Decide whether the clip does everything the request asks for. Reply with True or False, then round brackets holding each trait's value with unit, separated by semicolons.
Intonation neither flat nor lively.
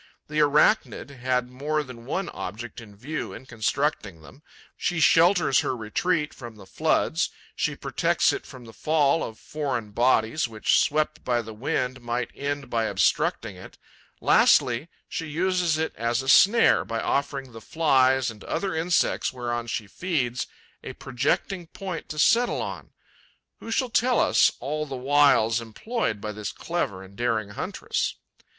True (4.9 semitones)